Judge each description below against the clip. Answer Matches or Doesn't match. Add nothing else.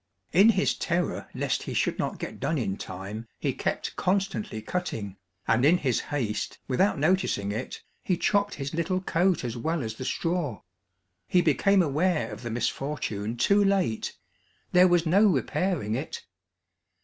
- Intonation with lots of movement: Matches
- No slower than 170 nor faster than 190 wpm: Doesn't match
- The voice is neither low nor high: Matches